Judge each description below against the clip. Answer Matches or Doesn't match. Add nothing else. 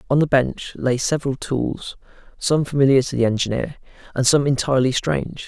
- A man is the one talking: Matches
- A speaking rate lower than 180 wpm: Matches